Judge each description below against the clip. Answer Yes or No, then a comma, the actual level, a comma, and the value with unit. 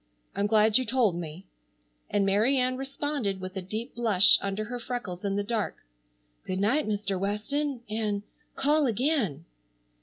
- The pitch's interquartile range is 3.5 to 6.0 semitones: Yes, average, 4.4 semitones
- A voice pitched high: Yes, high, 215 Hz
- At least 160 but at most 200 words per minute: No, average, 150 wpm